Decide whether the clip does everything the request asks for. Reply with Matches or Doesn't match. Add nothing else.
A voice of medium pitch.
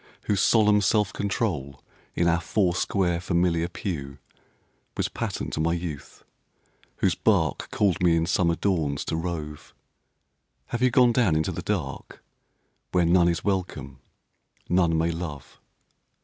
Doesn't match